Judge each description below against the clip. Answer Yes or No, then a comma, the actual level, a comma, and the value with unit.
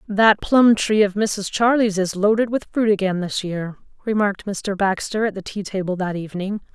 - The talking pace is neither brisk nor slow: Yes, average, 195 wpm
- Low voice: No, high, 200 Hz